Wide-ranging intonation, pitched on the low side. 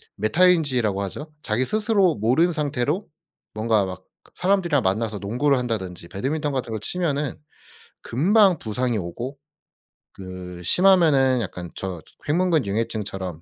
Yes: wide, 7.9 semitones; low, 125 Hz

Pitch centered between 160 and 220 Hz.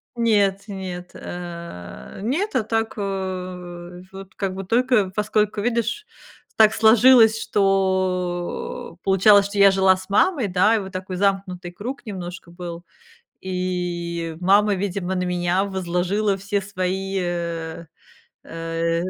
Yes: high, 190 Hz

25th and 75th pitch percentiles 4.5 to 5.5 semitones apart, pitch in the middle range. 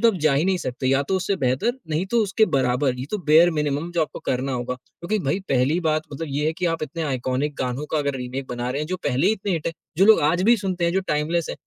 Yes: average, 4.9 semitones; medium, 155 Hz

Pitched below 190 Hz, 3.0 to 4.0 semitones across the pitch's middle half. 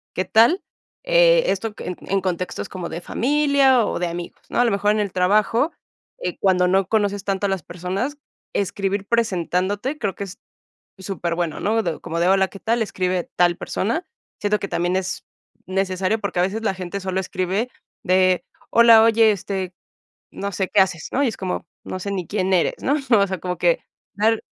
No: high, 195 Hz; average, 3.3 semitones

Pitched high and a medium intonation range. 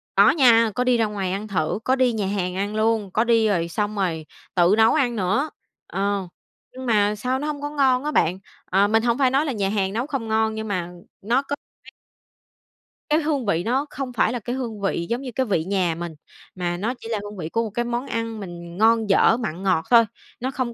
Yes: high, 220 Hz; average, 4.3 semitones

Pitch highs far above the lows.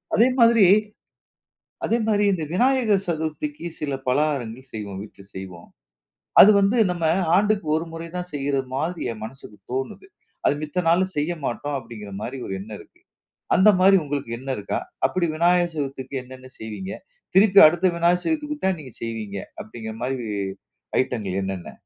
Yes: wide, 7.9 semitones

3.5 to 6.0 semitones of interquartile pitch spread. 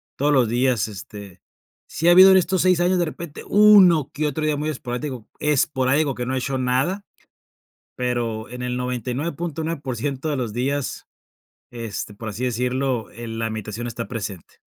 Yes: average, 4.4 semitones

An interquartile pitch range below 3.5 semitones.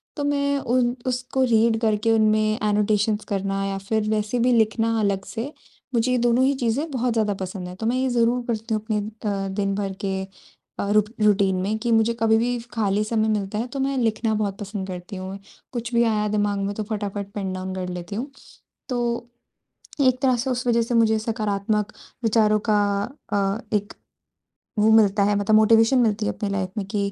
Yes: narrow, 2.6 semitones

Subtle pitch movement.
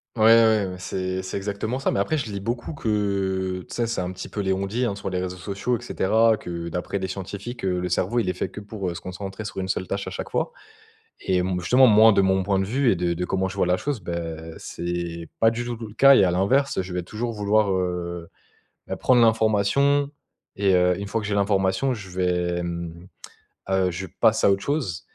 No: average, 3.4 semitones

